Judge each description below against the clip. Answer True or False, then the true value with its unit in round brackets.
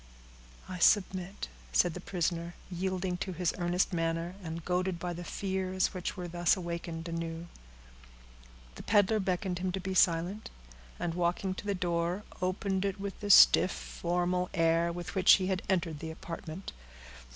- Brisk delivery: False (160 wpm)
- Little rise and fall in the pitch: True (1.8 semitones)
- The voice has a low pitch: False (180 Hz)